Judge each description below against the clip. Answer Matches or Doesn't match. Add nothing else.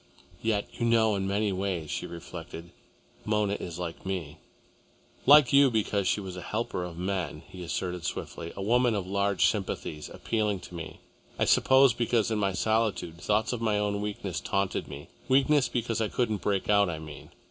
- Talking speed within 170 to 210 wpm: Matches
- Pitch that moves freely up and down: Doesn't match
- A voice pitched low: Matches